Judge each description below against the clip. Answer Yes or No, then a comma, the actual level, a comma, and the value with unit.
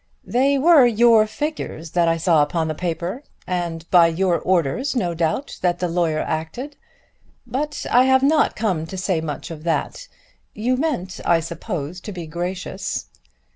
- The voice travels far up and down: Yes, wide, 6.8 semitones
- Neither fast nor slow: Yes, average, 165 wpm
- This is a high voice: No, medium, 180 Hz